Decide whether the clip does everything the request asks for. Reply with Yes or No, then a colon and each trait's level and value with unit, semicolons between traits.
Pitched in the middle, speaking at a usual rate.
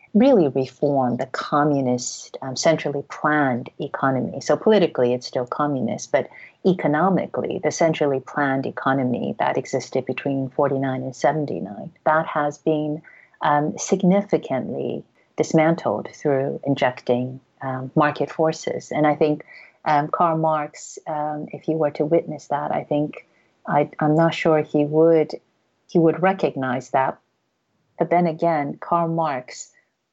No: medium, 150 Hz; slow, 130 wpm